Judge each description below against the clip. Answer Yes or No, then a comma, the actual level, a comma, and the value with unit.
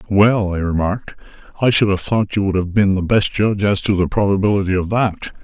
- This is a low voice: Yes, low, 100 Hz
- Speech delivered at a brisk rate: Yes, fast, 220 wpm